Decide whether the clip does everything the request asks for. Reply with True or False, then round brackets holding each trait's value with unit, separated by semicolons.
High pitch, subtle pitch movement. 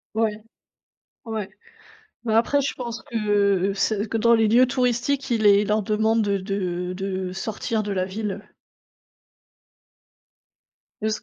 True (215 Hz; 2.3 semitones)